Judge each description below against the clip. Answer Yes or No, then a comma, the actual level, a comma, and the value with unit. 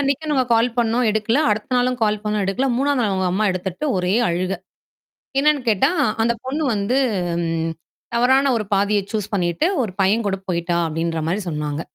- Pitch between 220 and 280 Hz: No, high, 210 Hz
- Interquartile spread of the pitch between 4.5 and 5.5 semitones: Yes, average, 5.1 semitones